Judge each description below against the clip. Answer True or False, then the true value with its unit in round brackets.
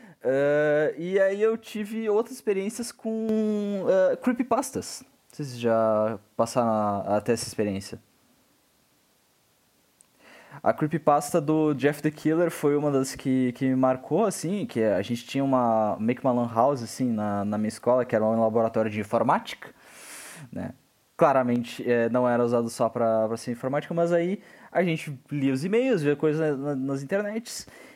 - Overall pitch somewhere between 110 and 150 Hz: True (135 Hz)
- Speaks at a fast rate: False (165 wpm)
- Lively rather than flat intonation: True (6.9 semitones)